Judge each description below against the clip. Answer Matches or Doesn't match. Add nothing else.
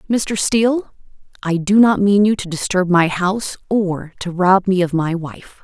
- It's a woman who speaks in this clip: Matches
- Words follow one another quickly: Doesn't match